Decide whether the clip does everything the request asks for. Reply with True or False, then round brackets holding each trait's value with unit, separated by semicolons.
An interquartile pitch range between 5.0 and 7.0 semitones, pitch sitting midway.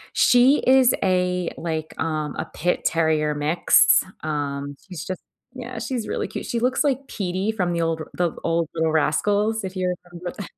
True (5.5 semitones; 180 Hz)